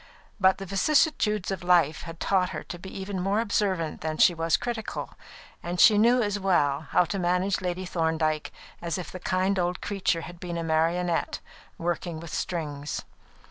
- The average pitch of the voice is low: No, medium, 180 Hz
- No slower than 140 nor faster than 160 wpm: No, average, 180 wpm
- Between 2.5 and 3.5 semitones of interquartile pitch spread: Yes, average, 2.8 semitones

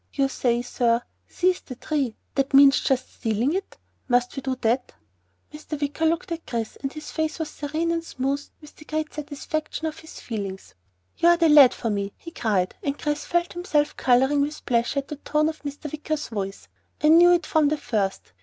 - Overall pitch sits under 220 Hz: No, very high, 290 Hz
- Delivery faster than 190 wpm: Yes, average, 200 wpm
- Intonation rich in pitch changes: No, average, 4.1 semitones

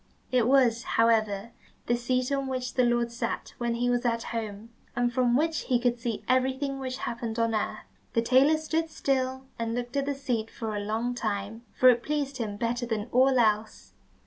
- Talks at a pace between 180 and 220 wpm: Yes, average, 200 wpm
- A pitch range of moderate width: No, narrow, 2.2 semitones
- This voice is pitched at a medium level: No, high, 240 Hz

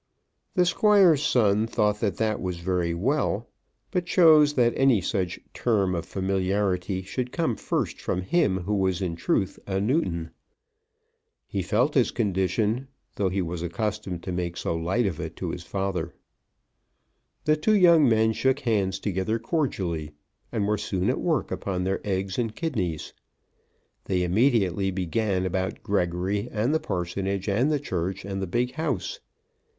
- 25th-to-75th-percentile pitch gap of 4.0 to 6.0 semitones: Yes, average, 4.7 semitones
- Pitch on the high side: No, low, 100 Hz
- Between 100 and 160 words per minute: Yes, average, 155 wpm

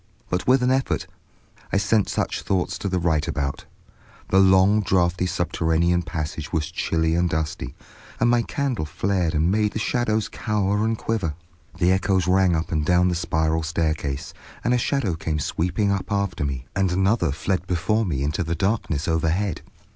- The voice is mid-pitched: No, very low, 90 Hz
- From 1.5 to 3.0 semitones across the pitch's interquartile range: No, average, 3.8 semitones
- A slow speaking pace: No, average, 175 wpm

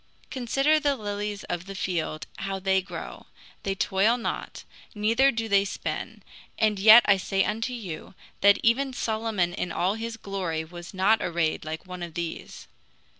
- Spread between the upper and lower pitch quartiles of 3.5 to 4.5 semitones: Yes, average, 3.8 semitones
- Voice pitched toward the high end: Yes, high, 200 Hz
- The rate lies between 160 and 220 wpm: Yes, average, 165 wpm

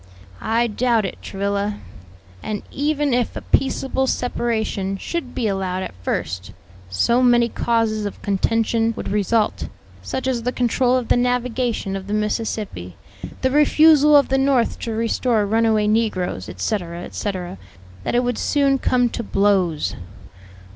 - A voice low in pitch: No, high, 225 Hz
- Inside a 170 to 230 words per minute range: No, average, 145 wpm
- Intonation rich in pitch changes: No, average, 3.8 semitones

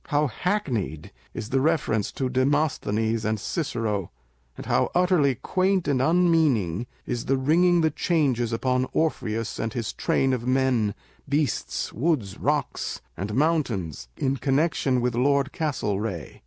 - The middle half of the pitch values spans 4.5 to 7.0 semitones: Yes, wide, 5.4 semitones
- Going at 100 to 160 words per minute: Yes, slow, 135 wpm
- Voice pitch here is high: No, low, 130 Hz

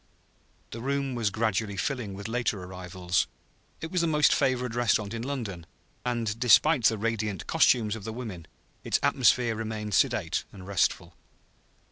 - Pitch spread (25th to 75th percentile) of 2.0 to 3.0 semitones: No, average, 3.6 semitones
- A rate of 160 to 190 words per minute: No, average, 150 wpm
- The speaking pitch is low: Yes, low, 110 Hz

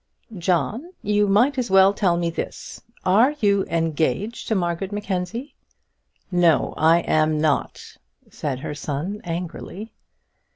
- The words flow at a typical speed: No, slow, 125 wpm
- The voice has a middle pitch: Yes, medium, 180 Hz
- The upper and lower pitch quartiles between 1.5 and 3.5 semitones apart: No, average, 4.1 semitones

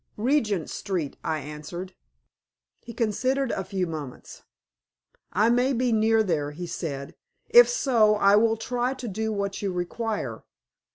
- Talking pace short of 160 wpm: Yes, average, 145 wpm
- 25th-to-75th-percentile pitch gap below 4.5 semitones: No, average, 5.0 semitones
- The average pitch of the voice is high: Yes, high, 210 Hz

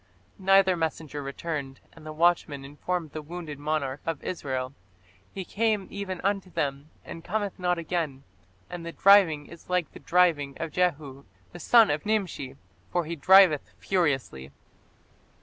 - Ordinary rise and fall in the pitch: Yes, average, 4.0 semitones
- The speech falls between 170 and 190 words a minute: No, average, 150 wpm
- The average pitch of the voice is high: No, medium, 165 Hz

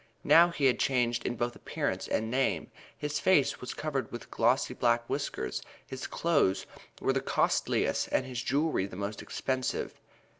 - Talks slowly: No, average, 160 wpm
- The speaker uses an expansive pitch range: No, average, 3.2 semitones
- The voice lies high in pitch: No, low, 125 Hz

